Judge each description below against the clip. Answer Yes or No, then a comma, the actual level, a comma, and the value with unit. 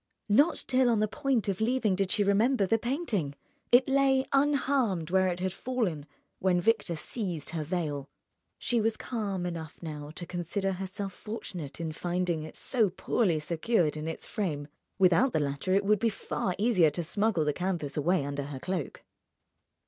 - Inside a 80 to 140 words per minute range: No, average, 175 wpm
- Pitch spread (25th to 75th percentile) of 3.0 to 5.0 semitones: No, wide, 5.6 semitones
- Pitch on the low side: No, high, 190 Hz